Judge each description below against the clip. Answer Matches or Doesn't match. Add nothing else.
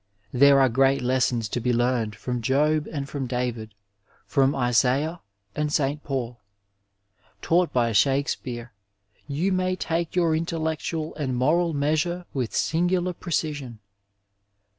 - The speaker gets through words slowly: Matches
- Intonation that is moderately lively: Matches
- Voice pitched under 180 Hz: Matches